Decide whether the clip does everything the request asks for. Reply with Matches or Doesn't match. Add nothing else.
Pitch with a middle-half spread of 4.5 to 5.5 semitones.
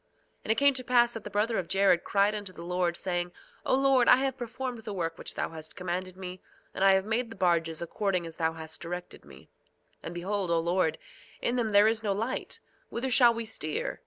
Matches